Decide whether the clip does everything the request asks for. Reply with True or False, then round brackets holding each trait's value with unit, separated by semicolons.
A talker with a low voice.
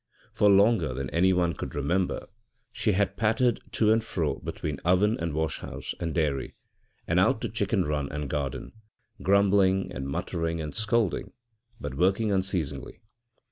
True (90 Hz)